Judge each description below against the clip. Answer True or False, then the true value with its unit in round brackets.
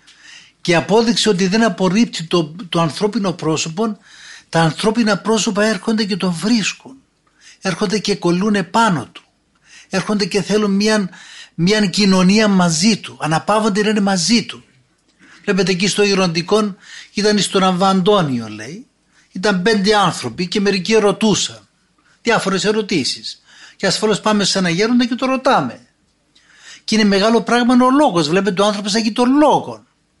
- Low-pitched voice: False (205 Hz)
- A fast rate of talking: False (135 wpm)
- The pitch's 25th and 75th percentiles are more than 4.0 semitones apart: False (2.7 semitones)